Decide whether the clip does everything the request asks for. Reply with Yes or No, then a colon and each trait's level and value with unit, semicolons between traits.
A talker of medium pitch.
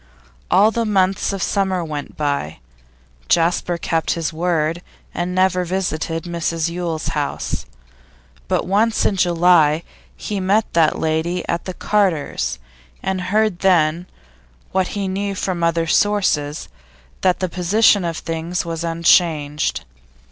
Yes: medium, 175 Hz